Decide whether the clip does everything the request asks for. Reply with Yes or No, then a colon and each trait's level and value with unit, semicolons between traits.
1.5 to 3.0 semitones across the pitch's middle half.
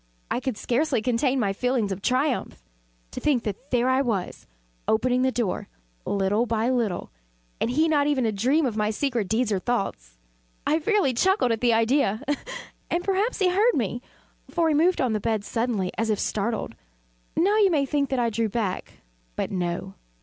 No: average, 4.9 semitones